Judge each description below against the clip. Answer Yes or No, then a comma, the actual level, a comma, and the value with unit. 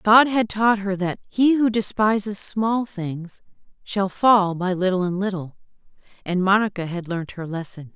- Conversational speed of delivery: Yes, average, 165 wpm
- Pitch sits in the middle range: No, high, 195 Hz